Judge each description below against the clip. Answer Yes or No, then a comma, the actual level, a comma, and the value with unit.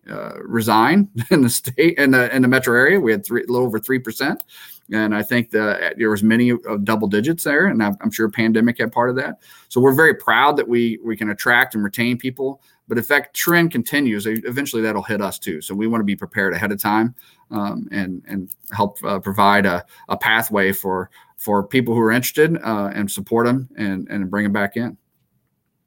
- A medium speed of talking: No, fast, 215 wpm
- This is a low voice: Yes, low, 110 Hz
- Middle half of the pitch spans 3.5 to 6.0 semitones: No, average, 2.9 semitones